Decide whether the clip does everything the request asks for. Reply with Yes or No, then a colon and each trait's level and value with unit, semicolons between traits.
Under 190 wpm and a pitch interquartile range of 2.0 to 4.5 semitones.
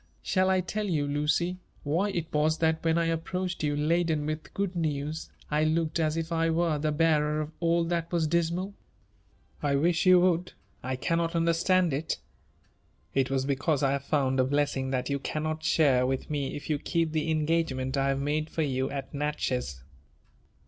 No: average, 195 wpm; average, 2.8 semitones